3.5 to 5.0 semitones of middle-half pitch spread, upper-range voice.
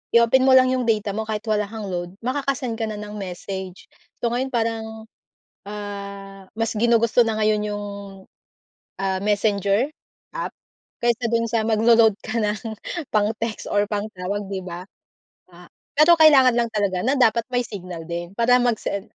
No: average, 2.8 semitones; high, 215 Hz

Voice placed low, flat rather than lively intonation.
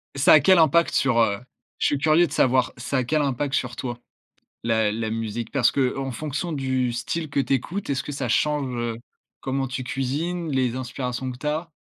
No: low, 130 Hz; average, 3.3 semitones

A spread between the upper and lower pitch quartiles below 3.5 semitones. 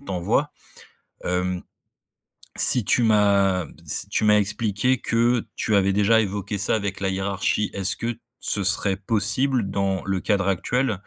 Yes: narrow, 2.5 semitones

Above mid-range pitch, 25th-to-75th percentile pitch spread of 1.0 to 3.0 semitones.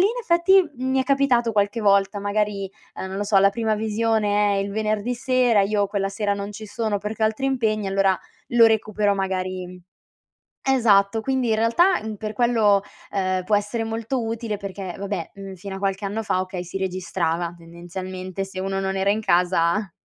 Yes: high, 205 Hz; narrow, 2.6 semitones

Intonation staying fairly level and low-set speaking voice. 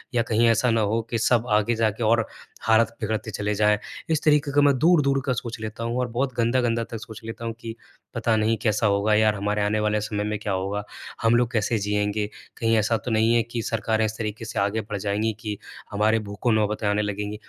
Yes: narrow, 1.8 semitones; low, 110 Hz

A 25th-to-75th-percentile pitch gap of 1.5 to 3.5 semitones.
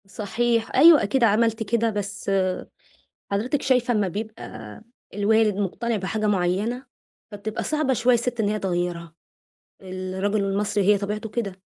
Yes: average, 2.9 semitones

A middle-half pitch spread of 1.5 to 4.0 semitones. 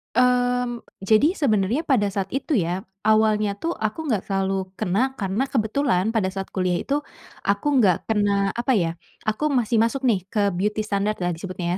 No: average, 4.4 semitones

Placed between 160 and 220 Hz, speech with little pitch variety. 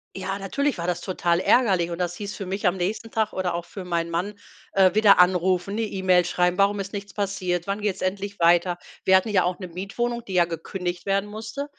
Yes: high, 190 Hz; narrow, 2.3 semitones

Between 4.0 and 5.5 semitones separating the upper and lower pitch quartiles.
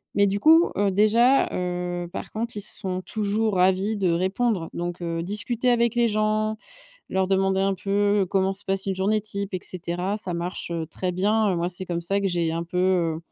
No: average, 2.9 semitones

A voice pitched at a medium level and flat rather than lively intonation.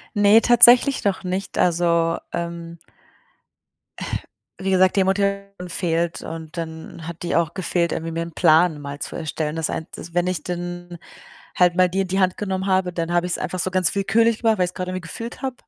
Yes: medium, 180 Hz; narrow, 2.3 semitones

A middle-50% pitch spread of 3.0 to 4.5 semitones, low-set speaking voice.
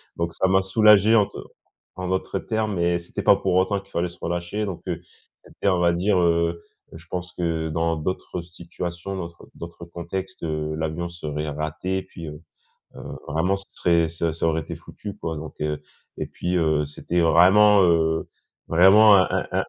No: narrow, 2.6 semitones; very low, 85 Hz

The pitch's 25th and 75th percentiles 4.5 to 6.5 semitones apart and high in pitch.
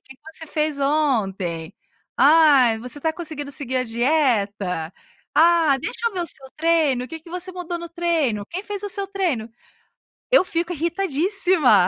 Yes: wide, 5.4 semitones; very high, 310 Hz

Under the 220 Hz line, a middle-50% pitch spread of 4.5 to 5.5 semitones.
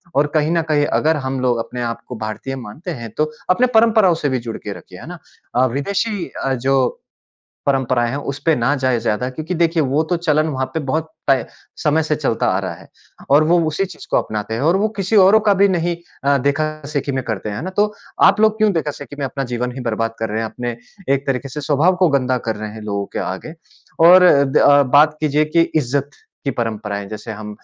Yes: medium, 140 Hz; average, 4.8 semitones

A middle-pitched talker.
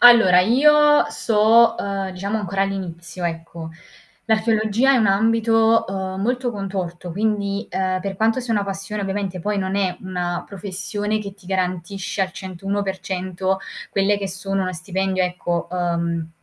No: high, 195 Hz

